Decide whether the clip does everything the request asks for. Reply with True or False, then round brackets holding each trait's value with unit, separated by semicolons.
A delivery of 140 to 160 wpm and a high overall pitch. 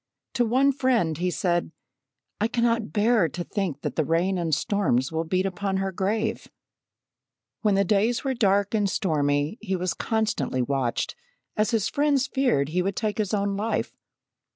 False (170 wpm; 200 Hz)